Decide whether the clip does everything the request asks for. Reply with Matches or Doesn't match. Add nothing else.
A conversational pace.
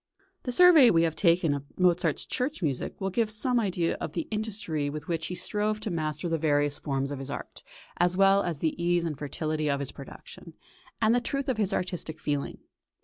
Doesn't match